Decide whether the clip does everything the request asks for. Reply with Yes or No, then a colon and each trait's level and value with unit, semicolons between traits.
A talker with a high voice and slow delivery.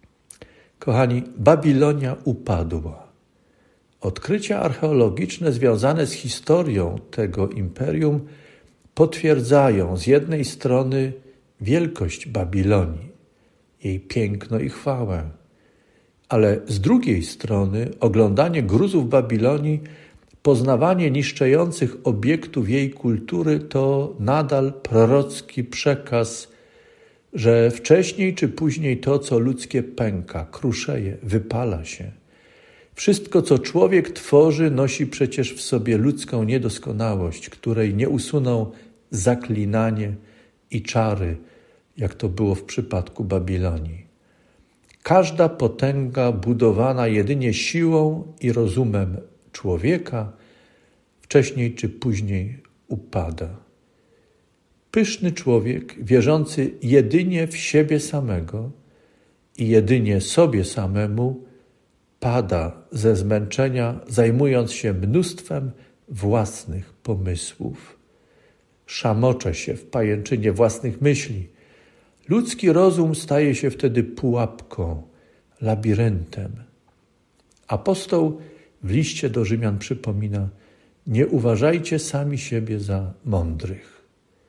No: low, 120 Hz; slow, 90 wpm